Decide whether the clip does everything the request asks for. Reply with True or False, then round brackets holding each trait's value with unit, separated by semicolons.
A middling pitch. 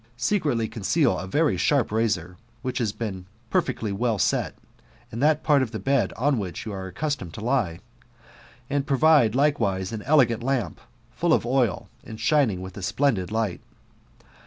False (115 Hz)